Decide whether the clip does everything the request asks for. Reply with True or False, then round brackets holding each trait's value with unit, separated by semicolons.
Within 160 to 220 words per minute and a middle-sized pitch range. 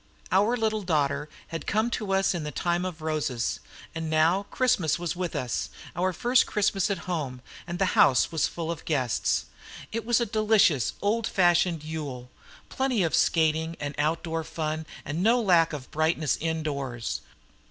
True (165 wpm; 4.1 semitones)